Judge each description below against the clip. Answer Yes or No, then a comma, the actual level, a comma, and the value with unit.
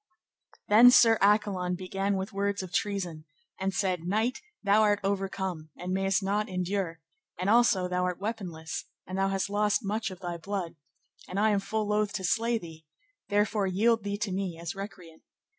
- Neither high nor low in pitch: No, high, 195 Hz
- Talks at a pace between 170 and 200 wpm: Yes, average, 175 wpm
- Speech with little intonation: Yes, narrow, 2.3 semitones